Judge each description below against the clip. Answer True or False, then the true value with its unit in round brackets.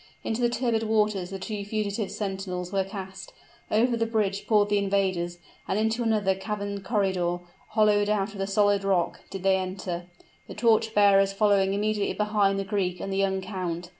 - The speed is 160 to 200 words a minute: True (180 wpm)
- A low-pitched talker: False (200 Hz)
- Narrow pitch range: True (1.8 semitones)